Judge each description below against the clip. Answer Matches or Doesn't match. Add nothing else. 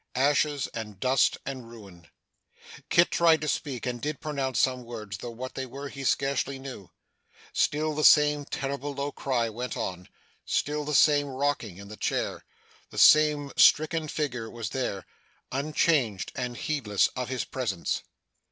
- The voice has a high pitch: Doesn't match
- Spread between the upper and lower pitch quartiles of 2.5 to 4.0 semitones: Matches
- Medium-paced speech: Matches